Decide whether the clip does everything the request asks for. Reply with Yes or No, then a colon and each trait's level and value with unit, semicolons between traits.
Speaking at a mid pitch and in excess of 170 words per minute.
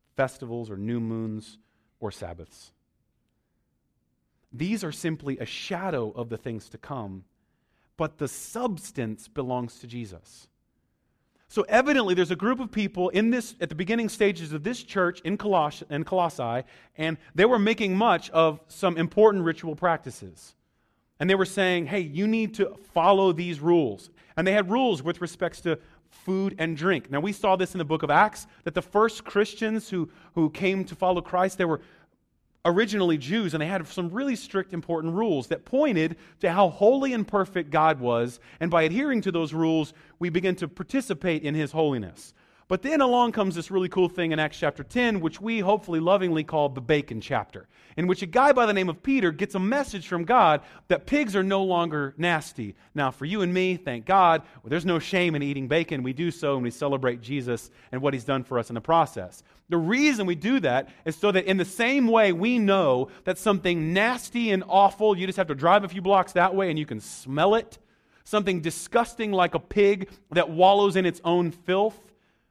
Yes: medium, 175 Hz; average, 200 wpm